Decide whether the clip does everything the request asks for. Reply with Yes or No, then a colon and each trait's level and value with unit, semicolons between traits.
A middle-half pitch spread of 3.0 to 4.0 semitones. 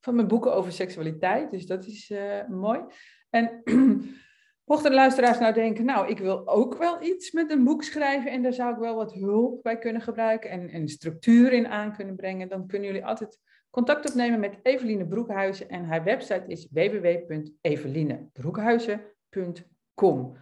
No: average, 4.6 semitones